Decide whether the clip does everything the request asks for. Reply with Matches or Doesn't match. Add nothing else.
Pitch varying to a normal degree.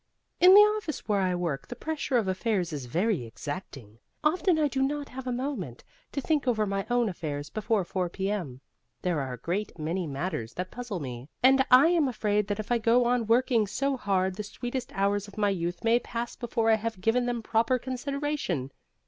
Doesn't match